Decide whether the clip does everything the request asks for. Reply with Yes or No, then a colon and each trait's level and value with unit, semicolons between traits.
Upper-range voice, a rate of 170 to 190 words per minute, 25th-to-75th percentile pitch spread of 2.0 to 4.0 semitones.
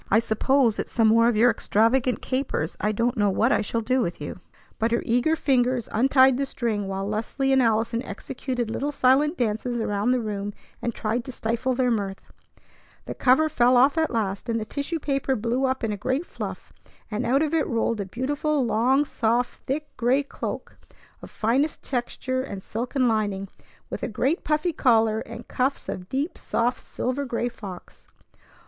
Yes: high, 240 Hz; average, 185 wpm; average, 3.4 semitones